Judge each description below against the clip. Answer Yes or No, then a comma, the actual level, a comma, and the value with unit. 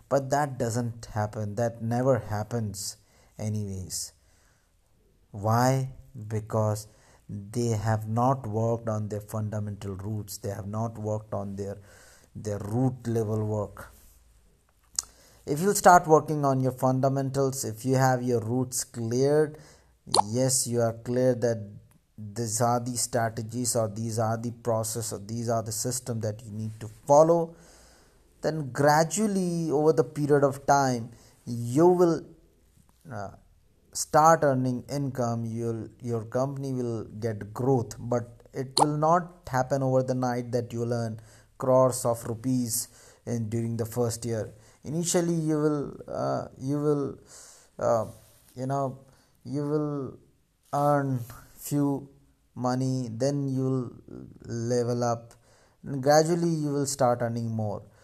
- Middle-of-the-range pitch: No, low, 120 Hz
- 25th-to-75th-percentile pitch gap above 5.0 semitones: No, average, 3.6 semitones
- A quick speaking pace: No, slow, 135 wpm